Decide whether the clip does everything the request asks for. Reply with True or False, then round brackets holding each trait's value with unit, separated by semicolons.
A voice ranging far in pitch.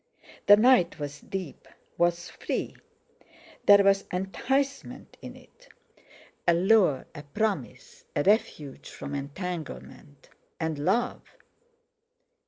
True (6.1 semitones)